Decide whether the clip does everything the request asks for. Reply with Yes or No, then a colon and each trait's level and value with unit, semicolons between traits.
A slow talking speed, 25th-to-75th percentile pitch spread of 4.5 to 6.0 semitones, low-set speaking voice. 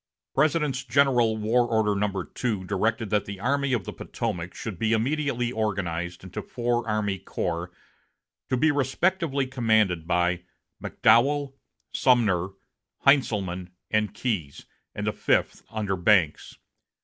Yes: slow, 125 wpm; average, 5.2 semitones; low, 110 Hz